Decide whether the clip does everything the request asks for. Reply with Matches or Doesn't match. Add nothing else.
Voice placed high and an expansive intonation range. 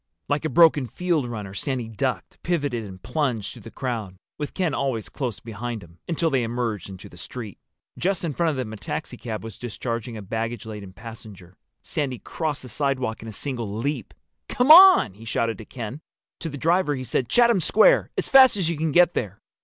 Doesn't match